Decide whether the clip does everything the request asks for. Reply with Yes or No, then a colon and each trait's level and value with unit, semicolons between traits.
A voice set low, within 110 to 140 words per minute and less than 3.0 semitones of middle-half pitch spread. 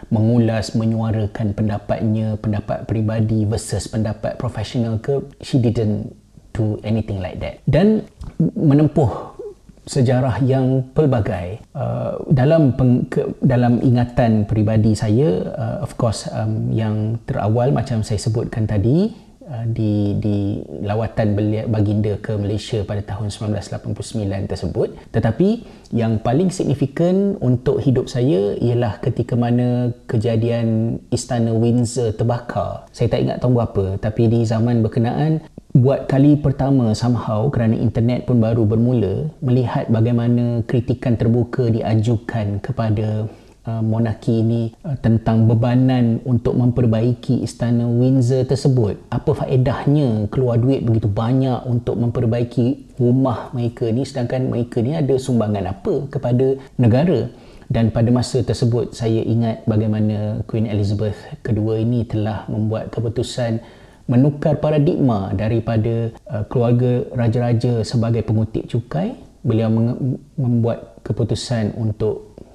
Yes: low, 115 Hz; average, 115 wpm; narrow, 2.6 semitones